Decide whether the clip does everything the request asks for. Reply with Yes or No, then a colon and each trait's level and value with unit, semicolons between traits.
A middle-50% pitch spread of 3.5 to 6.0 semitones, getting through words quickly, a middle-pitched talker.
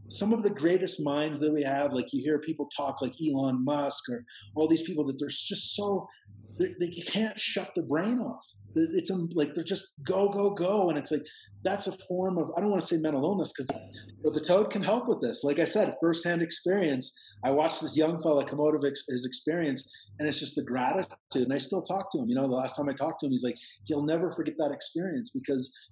Yes: average, 5.0 semitones; fast, 240 wpm; medium, 155 Hz